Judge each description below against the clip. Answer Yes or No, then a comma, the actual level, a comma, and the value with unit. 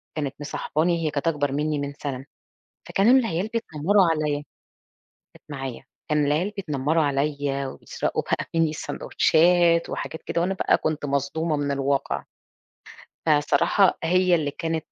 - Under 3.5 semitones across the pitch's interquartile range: Yes, average, 2.9 semitones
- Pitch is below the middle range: No, medium, 155 Hz